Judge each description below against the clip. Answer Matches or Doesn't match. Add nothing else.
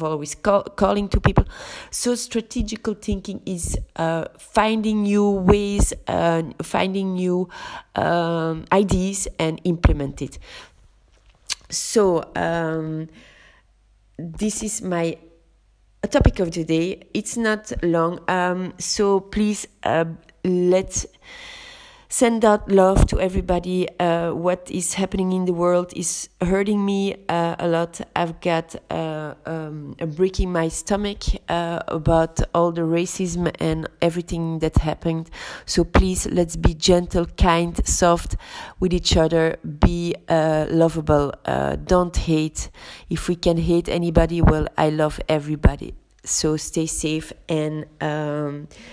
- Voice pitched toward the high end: Doesn't match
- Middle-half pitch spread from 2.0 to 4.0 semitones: Matches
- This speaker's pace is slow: Matches